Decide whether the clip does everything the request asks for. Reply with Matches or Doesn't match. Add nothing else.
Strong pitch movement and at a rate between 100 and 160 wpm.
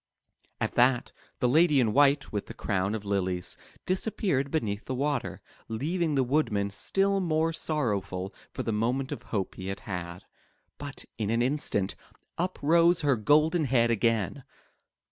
Matches